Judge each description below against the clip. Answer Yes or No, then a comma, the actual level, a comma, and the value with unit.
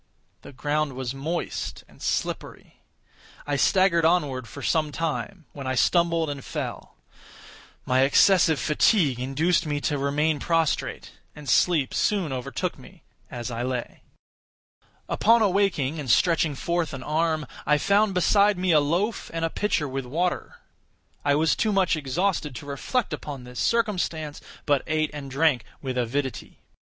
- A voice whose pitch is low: No, medium, 155 Hz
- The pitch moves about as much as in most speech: Yes, average, 4.2 semitones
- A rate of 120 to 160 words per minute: Yes, average, 150 wpm